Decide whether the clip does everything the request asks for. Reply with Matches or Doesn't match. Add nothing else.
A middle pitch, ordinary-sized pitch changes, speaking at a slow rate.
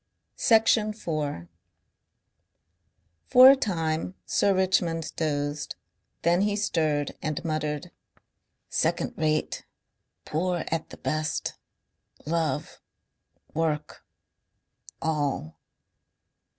Matches